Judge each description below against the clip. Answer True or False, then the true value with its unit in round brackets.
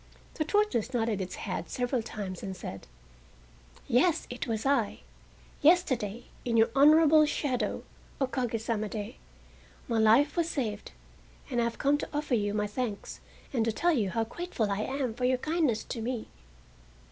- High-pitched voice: True (240 Hz)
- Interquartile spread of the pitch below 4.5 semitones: False (4.8 semitones)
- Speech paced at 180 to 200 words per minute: False (170 wpm)